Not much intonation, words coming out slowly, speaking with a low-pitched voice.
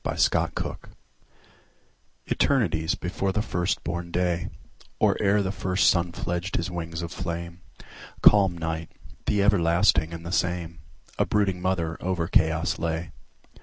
Yes: narrow, 2.0 semitones; slow, 125 wpm; very low, 85 Hz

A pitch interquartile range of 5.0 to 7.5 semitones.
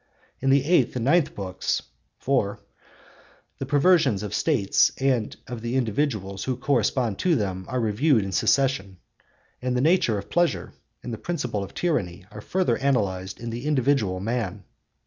Yes: wide, 5.6 semitones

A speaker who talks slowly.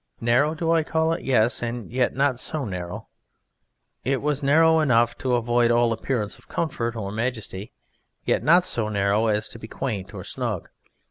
No: average, 180 wpm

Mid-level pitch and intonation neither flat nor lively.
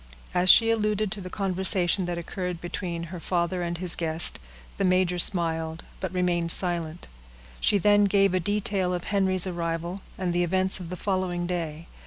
No: medium, 180 Hz; narrow, 1.8 semitones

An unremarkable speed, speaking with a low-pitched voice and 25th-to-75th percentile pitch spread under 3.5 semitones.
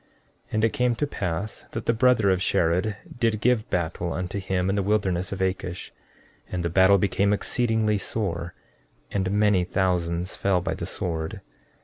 Yes: average, 170 wpm; very low, 95 Hz; average, 3.1 semitones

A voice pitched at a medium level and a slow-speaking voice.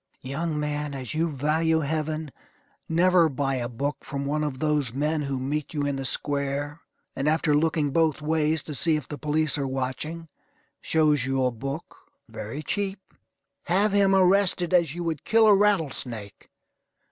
No: medium, 150 Hz; average, 170 wpm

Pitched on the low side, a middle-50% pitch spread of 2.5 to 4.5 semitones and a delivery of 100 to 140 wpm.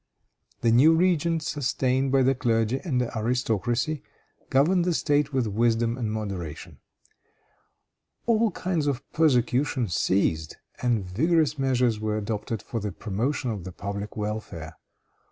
No: low, 120 Hz; average, 5.2 semitones; slow, 135 wpm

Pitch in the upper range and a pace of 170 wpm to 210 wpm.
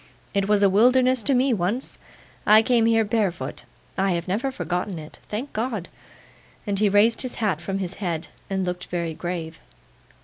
Yes: high, 200 Hz; average, 175 wpm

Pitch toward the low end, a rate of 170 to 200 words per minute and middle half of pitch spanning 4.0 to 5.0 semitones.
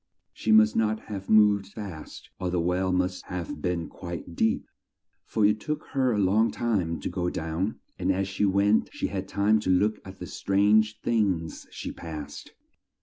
No: very low, 95 Hz; average, 180 wpm; average, 3.1 semitones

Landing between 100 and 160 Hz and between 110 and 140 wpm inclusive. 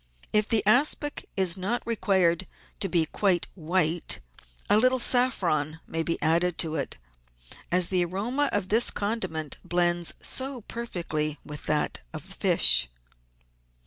No: medium, 185 Hz; slow, 135 wpm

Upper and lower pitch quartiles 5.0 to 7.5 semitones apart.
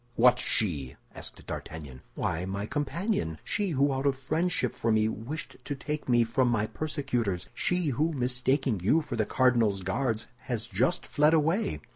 Yes: wide, 5.5 semitones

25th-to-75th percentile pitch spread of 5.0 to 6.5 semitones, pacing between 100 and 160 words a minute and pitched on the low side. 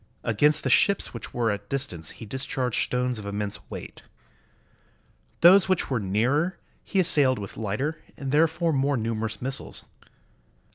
Yes: wide, 5.5 semitones; average, 150 wpm; low, 130 Hz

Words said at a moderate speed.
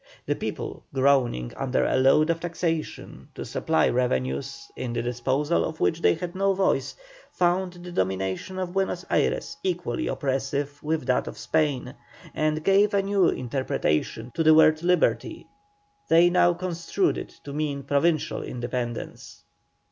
Yes: average, 150 wpm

